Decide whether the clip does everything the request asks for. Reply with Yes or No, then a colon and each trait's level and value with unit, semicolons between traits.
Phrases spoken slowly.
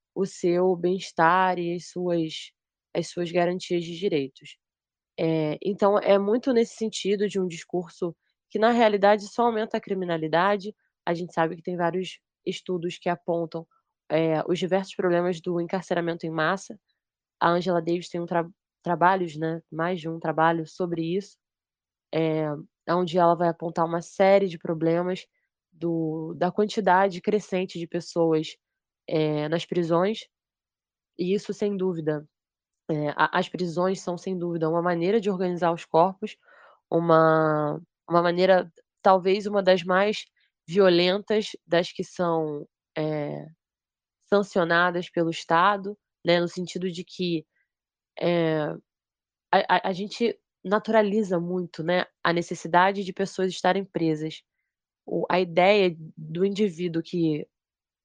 No: average, 135 wpm